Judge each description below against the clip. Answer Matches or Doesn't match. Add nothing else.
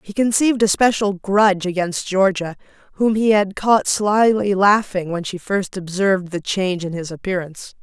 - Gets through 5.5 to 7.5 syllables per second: Doesn't match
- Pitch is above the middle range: Matches